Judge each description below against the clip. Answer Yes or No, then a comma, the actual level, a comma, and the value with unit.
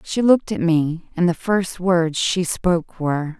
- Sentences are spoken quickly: No, average, 195 wpm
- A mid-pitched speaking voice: Yes, medium, 175 Hz